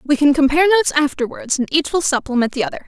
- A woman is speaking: Yes, female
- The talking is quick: Yes, fast, 230 wpm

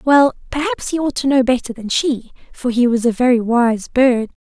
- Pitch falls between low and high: No, very high, 255 Hz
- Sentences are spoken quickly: Yes, fast, 215 wpm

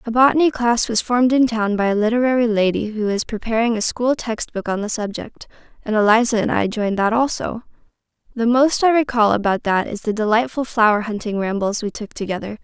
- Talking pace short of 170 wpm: No, fast, 205 wpm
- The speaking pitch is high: Yes, high, 225 Hz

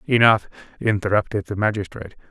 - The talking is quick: No, slow, 105 wpm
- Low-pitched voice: Yes, low, 100 Hz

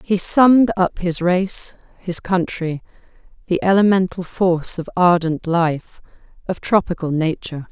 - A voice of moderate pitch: Yes, medium, 180 Hz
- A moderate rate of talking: No, slow, 125 wpm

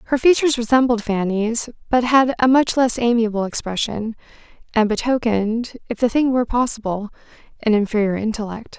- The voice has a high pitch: Yes, high, 230 Hz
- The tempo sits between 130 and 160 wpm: Yes, average, 145 wpm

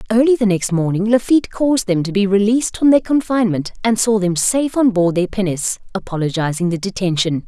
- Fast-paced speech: No, average, 195 wpm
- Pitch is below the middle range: No, high, 205 Hz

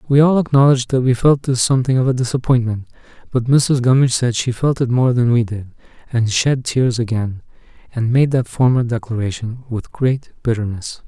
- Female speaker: No, male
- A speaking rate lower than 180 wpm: No, average, 185 wpm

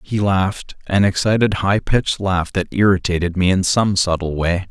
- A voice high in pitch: No, very low, 95 Hz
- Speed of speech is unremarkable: Yes, average, 180 wpm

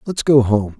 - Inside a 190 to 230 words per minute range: Yes, fast, 225 wpm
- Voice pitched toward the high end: No, low, 125 Hz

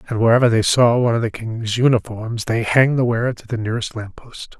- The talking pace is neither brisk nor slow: No, fast, 235 wpm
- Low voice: Yes, low, 115 Hz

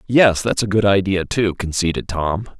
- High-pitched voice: No, very low, 95 Hz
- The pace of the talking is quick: No, average, 185 wpm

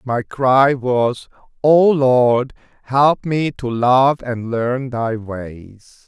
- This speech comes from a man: Yes, male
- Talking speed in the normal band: No, slow, 130 wpm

